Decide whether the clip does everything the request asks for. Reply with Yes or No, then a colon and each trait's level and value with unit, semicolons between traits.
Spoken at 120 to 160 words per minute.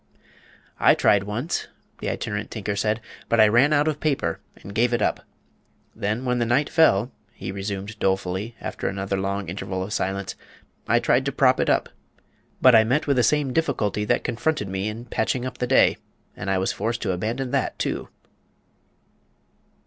No: average, 180 wpm